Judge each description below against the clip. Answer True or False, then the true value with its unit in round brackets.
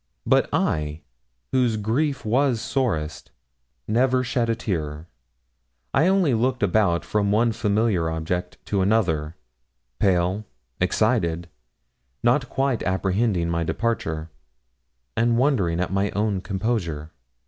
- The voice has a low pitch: True (105 Hz)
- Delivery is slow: True (115 wpm)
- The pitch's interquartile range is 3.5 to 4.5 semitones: False (5.6 semitones)